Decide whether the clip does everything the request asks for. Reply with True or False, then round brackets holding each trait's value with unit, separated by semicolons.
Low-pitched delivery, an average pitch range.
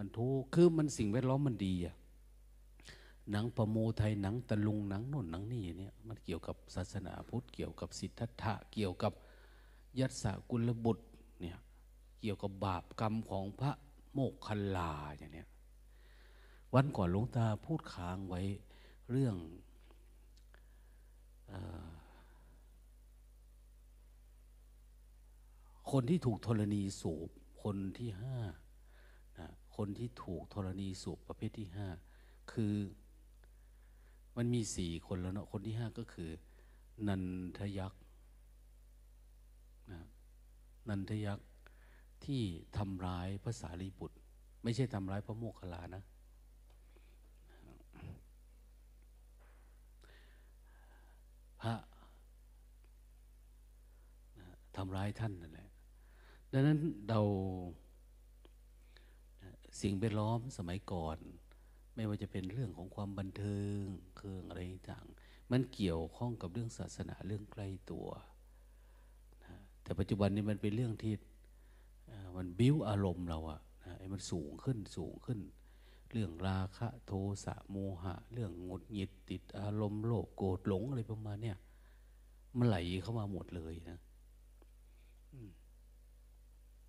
True (95 Hz; 4.9 semitones)